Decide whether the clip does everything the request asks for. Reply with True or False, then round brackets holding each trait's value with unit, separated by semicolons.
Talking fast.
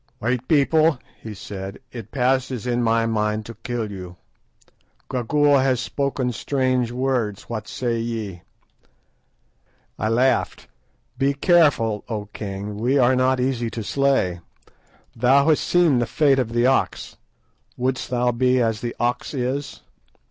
False (140 wpm)